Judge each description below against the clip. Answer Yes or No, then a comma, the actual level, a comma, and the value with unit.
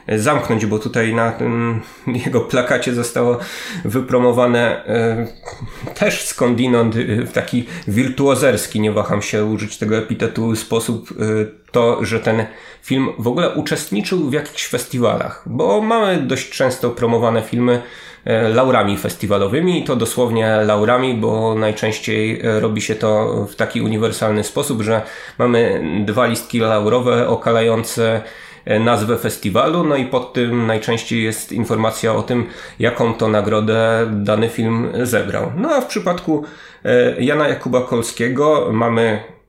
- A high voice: No, low, 115 Hz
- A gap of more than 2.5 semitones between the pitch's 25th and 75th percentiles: No, narrow, 2.0 semitones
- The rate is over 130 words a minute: No, average, 125 wpm